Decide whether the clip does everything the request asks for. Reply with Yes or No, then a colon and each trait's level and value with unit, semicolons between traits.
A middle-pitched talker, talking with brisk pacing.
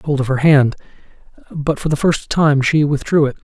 Yes: medium, 145 Hz; fast, 240 wpm